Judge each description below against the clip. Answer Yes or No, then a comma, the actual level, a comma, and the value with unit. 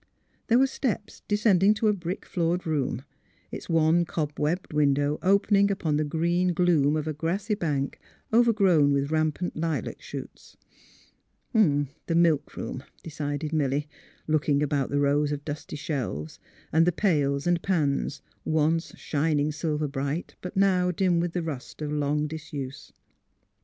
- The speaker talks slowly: No, average, 150 wpm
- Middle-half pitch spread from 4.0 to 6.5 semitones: No, average, 3.5 semitones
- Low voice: No, medium, 155 Hz